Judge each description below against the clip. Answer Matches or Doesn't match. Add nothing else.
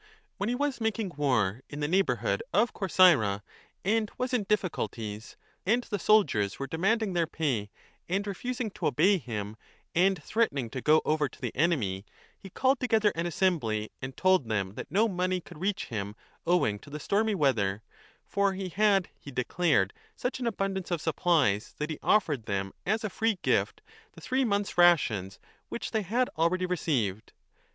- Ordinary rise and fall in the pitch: Doesn't match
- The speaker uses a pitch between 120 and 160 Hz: Doesn't match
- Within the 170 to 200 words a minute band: Matches